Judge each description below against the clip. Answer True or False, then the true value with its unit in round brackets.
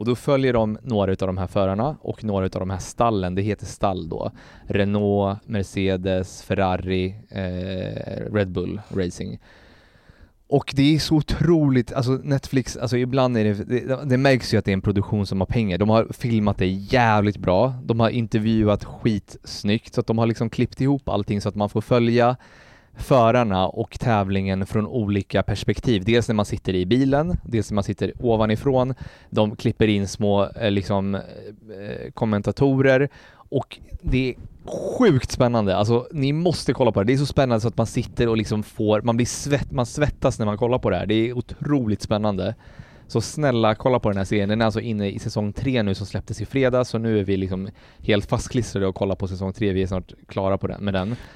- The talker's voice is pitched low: True (110 Hz)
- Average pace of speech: False (200 wpm)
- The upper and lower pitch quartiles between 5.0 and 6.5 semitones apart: False (3.8 semitones)